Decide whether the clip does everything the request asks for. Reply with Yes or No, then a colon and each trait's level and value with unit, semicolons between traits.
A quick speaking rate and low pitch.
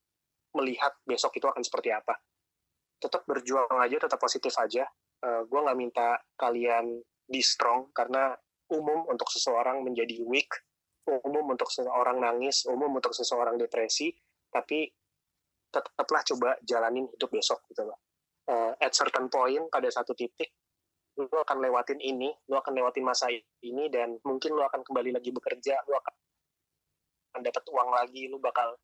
Yes: fast, 145 wpm; low, 130 Hz